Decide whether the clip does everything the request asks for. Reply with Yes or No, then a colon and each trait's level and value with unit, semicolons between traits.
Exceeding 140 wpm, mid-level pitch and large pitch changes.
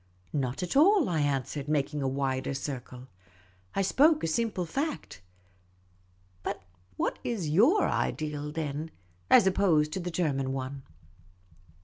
No: slow, 135 wpm; medium, 150 Hz; wide, 5.8 semitones